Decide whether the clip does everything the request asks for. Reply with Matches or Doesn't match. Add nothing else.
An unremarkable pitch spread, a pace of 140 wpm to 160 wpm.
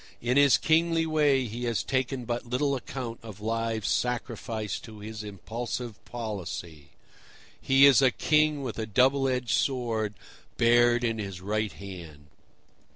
Matches